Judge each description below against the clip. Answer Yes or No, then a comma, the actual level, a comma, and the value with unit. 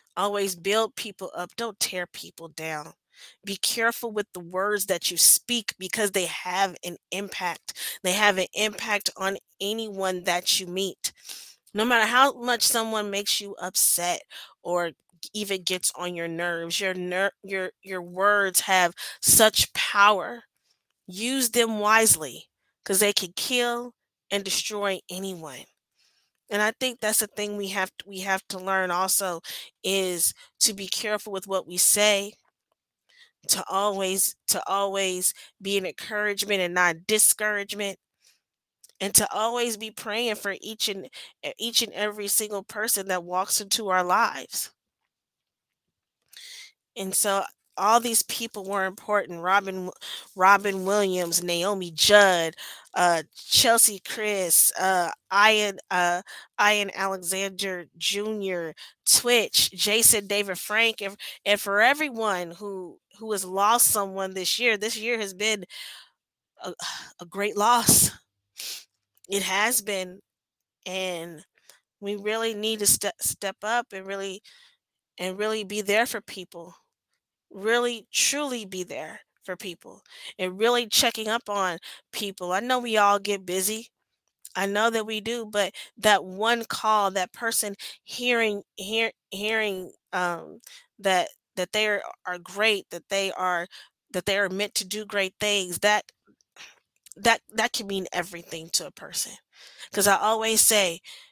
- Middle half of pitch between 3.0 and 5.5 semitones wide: No, narrow, 2.6 semitones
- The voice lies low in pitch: No, high, 200 Hz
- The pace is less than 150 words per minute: Yes, average, 140 wpm